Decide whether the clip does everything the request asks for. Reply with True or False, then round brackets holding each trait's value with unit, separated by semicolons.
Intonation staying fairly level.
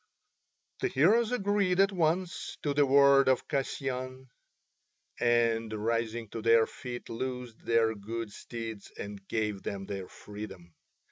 False (4.0 semitones)